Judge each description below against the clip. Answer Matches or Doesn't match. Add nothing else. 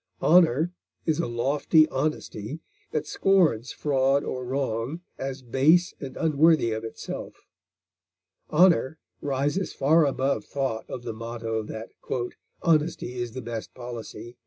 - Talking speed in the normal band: Doesn't match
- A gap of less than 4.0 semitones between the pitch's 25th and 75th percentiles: Doesn't match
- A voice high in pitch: Doesn't match